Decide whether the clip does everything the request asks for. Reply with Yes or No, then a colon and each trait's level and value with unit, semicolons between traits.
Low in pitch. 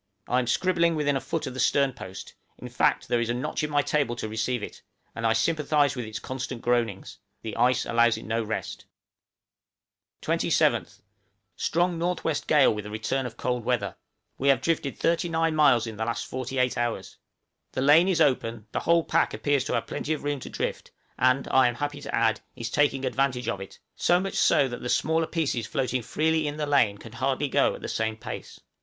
Yes: low, 130 Hz